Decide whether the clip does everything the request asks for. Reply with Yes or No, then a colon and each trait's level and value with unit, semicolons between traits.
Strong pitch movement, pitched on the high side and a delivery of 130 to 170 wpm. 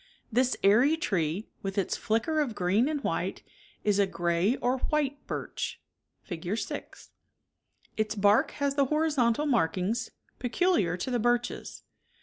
Yes: wide, 6.0 semitones; high, 230 Hz; average, 140 wpm